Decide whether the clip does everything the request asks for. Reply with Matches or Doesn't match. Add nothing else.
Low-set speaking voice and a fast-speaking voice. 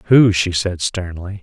Doesn't match